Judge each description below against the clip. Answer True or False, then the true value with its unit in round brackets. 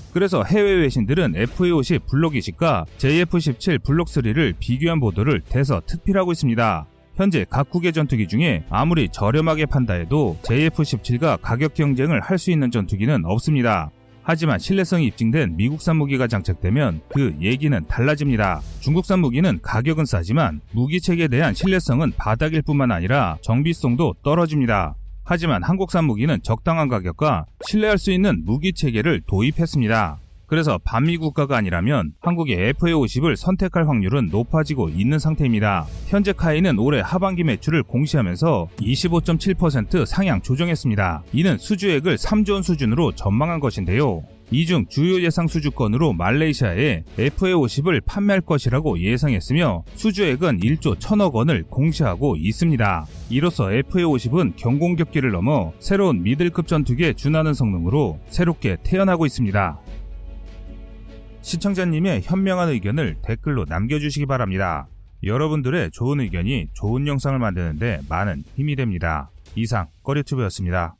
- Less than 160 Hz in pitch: True (140 Hz)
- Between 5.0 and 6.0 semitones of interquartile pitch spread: False (7.4 semitones)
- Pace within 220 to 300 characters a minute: False (345 characters per minute)